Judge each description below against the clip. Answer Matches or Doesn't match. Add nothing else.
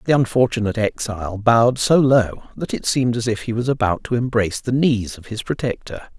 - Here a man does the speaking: Matches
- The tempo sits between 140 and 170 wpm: Doesn't match